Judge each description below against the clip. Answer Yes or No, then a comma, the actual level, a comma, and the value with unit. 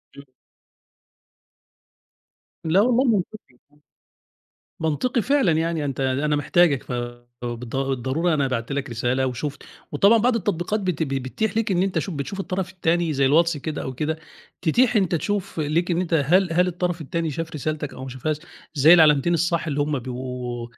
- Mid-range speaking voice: Yes, medium, 160 Hz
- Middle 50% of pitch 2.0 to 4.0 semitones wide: No, average, 4.8 semitones